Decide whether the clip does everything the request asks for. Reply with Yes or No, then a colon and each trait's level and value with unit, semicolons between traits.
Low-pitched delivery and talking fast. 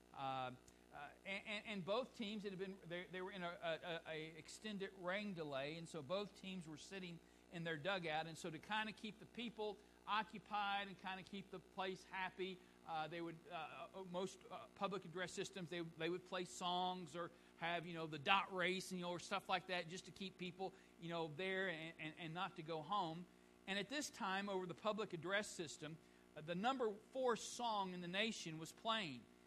No: medium, 185 Hz; fast, 210 wpm